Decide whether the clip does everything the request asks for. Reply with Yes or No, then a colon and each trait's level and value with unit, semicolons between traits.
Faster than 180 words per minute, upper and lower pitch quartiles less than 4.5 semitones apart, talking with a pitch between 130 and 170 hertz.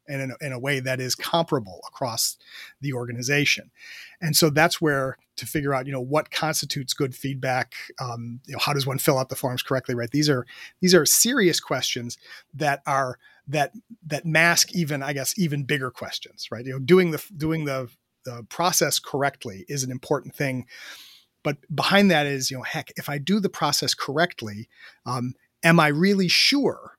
Yes: average, 190 wpm; average, 3.6 semitones; medium, 140 Hz